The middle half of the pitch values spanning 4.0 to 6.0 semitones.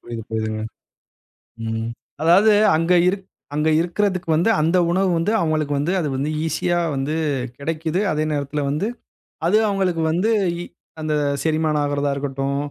No: average, 3.6 semitones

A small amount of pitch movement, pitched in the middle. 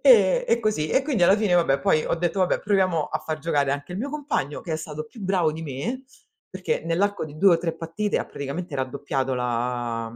No: wide, 5.9 semitones; medium, 165 Hz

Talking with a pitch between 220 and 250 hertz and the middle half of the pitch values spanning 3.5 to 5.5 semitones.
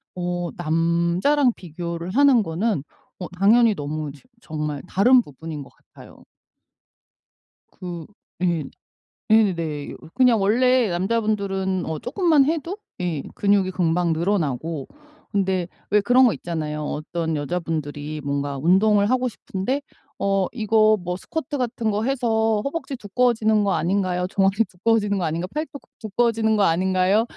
No: high, 190 Hz; average, 5.2 semitones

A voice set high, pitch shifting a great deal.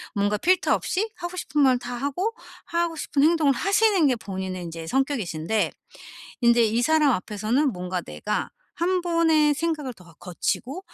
Yes: very high, 270 Hz; wide, 8.0 semitones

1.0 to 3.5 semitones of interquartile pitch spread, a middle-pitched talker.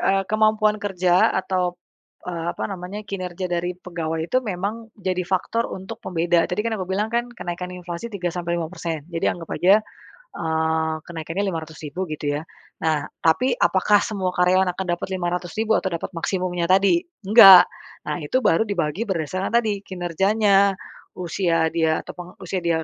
Yes: average, 2.8 semitones; medium, 180 Hz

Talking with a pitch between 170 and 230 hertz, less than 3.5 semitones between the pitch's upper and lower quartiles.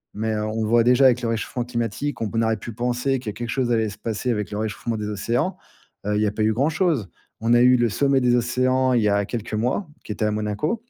No: low, 115 Hz; average, 2.9 semitones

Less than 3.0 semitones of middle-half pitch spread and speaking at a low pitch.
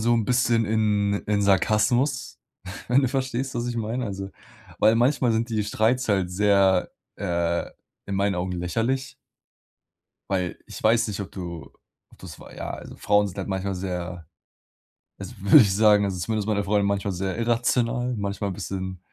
No: average, 3.5 semitones; low, 105 Hz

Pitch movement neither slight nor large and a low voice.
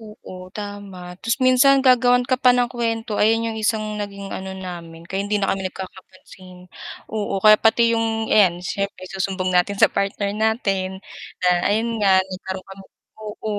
No: average, 3.0 semitones; high, 205 Hz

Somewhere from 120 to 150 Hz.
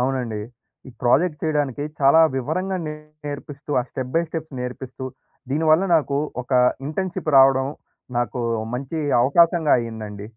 Yes: medium, 140 Hz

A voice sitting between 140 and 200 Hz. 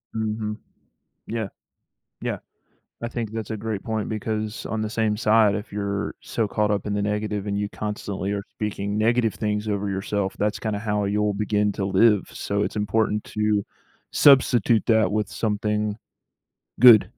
No: low, 105 Hz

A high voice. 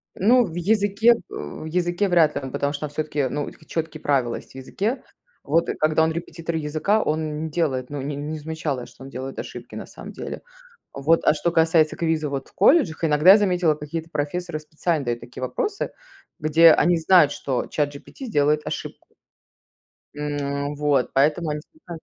No: medium, 155 Hz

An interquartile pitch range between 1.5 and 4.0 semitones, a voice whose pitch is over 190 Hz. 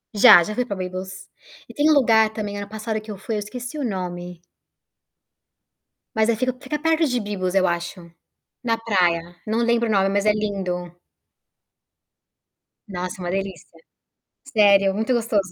Yes: average, 3.7 semitones; high, 205 Hz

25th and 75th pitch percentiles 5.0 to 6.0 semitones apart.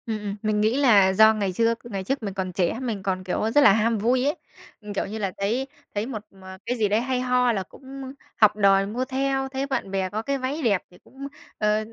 No: average, 4.1 semitones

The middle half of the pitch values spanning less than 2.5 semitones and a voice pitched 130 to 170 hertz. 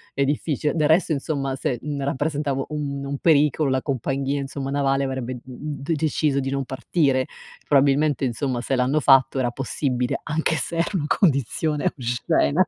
Yes: narrow, 2.1 semitones; medium, 140 Hz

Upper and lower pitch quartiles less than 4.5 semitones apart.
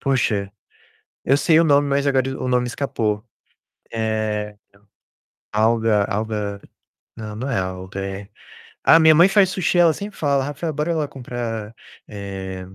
No: wide, 5.5 semitones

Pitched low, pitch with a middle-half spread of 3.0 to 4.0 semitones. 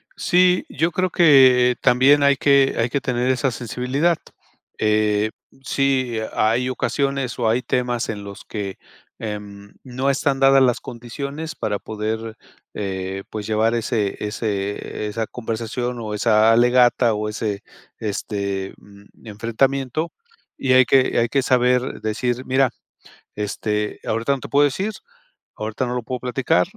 Yes: low, 120 Hz; average, 3.7 semitones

